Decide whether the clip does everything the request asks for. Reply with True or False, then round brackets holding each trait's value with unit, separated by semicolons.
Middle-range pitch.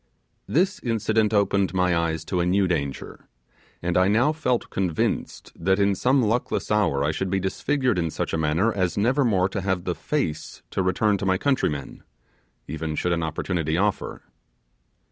False (95 Hz)